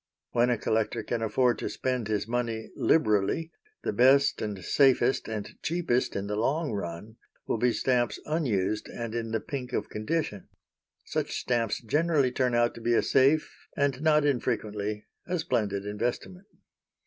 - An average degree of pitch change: Yes, average, 4.3 semitones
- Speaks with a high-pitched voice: No, low, 120 Hz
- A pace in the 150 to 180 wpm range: Yes, average, 160 wpm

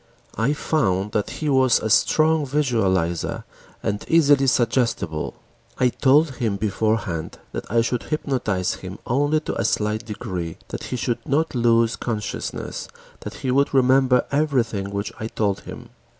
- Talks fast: No, average, 150 wpm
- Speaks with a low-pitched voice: Yes, low, 120 Hz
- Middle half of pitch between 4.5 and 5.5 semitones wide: Yes, average, 5.0 semitones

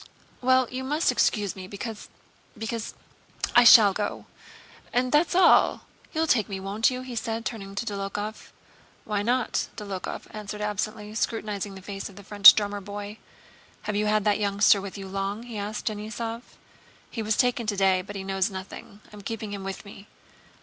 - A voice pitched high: Yes, high, 210 Hz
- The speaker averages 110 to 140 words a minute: No, average, 175 wpm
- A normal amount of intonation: No, narrow, 2.2 semitones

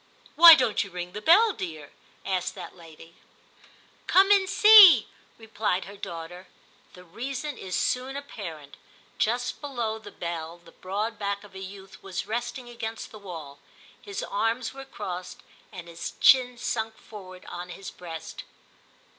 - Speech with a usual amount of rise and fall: No, wide, 5.8 semitones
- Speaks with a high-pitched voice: Yes, high, 205 Hz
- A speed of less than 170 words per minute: Yes, average, 160 wpm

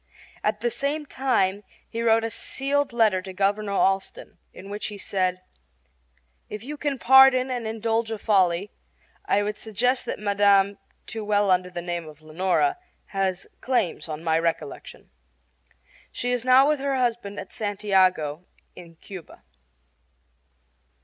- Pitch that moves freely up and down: No, average, 4.5 semitones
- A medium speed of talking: Yes, average, 150 wpm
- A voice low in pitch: No, high, 205 Hz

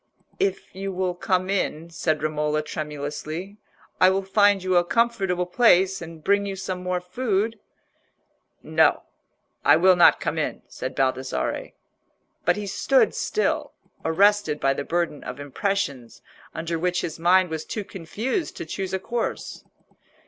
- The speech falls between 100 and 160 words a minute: Yes, average, 150 wpm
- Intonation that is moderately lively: Yes, average, 3.6 semitones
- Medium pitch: Yes, medium, 180 Hz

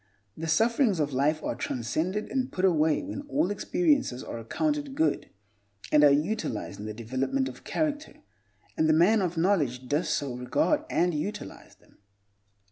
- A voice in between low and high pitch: Yes, medium, 170 Hz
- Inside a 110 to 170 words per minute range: Yes, average, 160 wpm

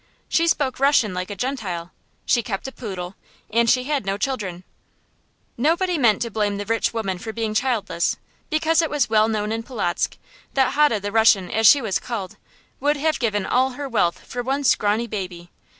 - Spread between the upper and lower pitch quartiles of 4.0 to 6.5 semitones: Yes, average, 4.8 semitones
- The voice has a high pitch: Yes, high, 225 Hz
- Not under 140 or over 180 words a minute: No, average, 190 wpm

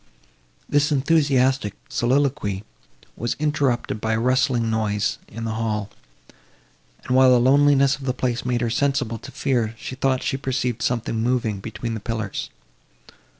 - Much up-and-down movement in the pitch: No, average, 3.2 semitones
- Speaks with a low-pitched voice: Yes, low, 125 Hz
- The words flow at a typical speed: Yes, average, 150 wpm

